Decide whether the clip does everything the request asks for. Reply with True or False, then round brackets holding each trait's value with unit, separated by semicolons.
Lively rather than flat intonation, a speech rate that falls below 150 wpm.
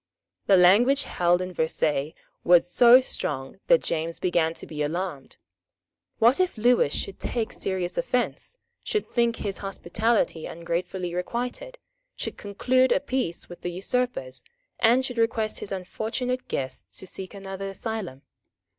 True (5.7 semitones; 140 wpm)